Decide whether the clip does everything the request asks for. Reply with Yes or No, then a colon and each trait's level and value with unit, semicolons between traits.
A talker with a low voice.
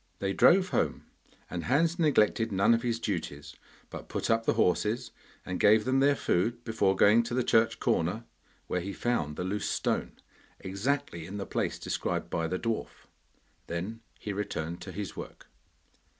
Yes: low, 105 Hz